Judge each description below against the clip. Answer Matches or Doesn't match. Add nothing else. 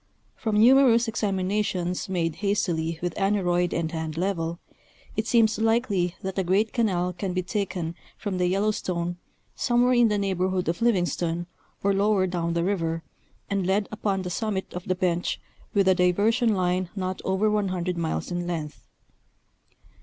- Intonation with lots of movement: Doesn't match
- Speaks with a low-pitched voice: Doesn't match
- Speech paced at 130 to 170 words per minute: Matches